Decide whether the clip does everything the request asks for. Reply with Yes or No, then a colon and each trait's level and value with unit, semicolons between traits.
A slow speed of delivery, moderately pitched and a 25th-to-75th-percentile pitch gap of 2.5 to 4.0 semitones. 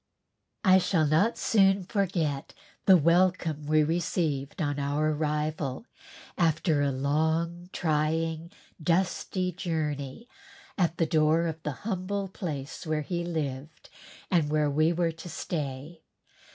Yes: slow, 125 wpm; medium, 160 Hz; average, 2.8 semitones